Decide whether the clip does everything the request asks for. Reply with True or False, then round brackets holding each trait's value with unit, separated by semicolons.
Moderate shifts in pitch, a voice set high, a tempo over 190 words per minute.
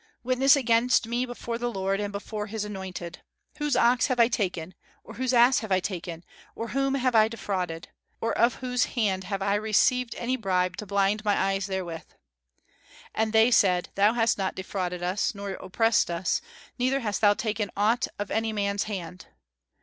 False (3.7 semitones; 210 Hz; 180 wpm)